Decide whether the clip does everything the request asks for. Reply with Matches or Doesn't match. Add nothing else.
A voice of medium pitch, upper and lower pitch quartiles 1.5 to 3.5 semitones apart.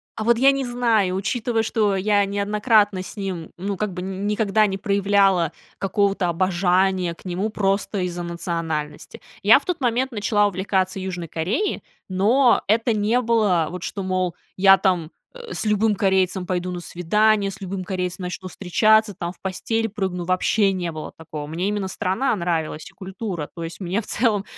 Doesn't match